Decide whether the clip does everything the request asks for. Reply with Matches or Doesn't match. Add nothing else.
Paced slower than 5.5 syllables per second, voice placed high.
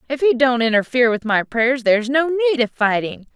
Doesn't match